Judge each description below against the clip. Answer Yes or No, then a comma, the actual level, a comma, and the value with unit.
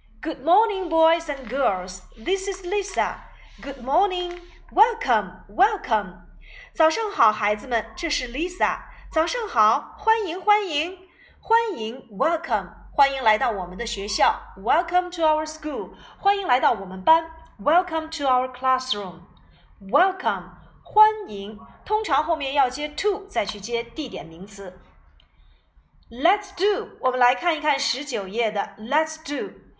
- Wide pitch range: Yes, wide, 8.2 semitones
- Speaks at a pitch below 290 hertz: No, very high, 305 Hz